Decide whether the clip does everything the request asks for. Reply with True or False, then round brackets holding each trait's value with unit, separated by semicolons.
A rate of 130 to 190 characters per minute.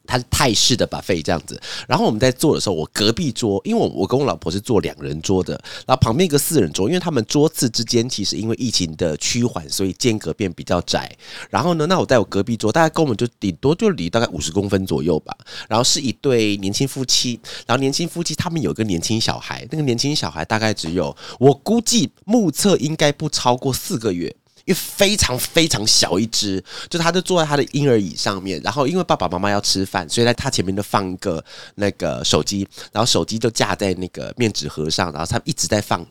False (355 characters per minute)